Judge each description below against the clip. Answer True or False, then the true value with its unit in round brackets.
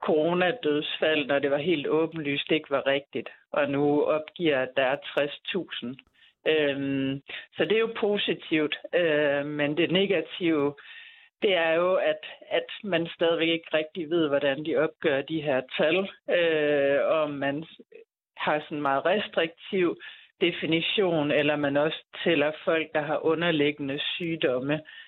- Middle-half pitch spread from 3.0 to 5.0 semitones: True (3.3 semitones)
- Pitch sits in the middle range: True (155 Hz)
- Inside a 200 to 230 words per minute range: False (145 wpm)